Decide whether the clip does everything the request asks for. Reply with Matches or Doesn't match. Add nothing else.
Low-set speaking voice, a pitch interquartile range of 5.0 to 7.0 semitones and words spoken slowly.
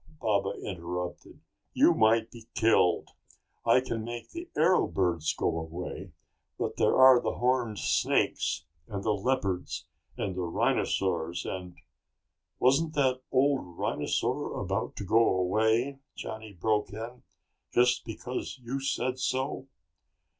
Matches